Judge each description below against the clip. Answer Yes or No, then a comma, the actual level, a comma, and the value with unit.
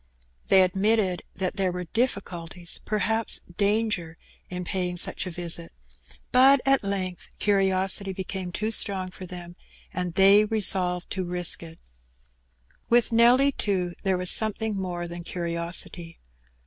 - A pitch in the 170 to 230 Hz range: Yes, medium, 185 Hz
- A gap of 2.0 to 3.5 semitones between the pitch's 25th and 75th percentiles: Yes, average, 2.9 semitones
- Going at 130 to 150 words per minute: Yes, slow, 135 wpm